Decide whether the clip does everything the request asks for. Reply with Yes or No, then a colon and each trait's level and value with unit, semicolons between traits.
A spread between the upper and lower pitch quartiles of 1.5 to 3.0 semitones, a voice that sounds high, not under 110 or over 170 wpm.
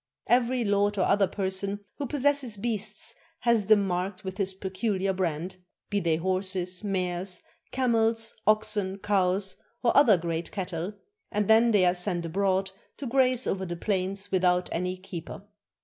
Yes: average, 2.7 semitones; high, 195 Hz; average, 150 wpm